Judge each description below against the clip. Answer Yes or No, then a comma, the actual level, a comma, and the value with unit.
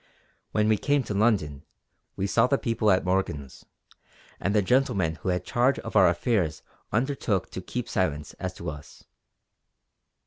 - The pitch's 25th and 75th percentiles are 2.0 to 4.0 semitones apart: No, average, 5.1 semitones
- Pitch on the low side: Yes, low, 100 Hz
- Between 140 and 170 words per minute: Yes, average, 160 wpm